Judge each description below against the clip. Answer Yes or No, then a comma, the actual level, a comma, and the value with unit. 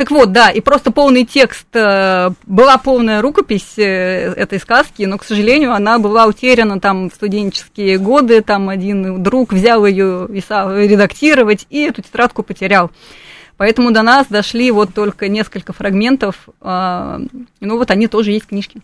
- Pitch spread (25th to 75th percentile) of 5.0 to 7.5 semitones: No, average, 3.6 semitones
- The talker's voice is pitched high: Yes, high, 210 Hz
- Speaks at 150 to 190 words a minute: Yes, average, 155 wpm